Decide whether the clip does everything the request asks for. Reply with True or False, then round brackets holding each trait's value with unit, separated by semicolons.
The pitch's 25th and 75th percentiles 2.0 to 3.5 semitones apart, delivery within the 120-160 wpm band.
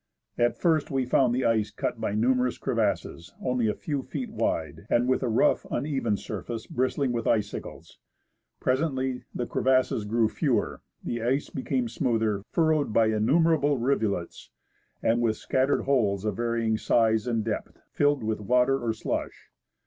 True (3.2 semitones; 155 wpm)